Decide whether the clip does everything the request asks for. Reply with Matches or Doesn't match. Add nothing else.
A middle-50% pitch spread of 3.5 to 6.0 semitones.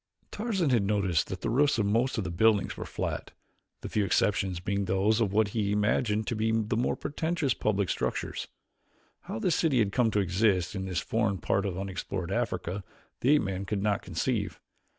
Doesn't match